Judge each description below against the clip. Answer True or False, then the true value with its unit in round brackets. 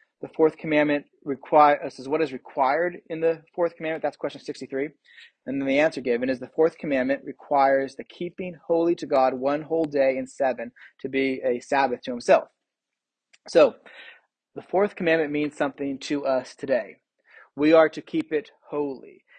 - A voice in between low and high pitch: True (150 Hz)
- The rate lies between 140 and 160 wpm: False (175 wpm)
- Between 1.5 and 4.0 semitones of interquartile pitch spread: True (3.2 semitones)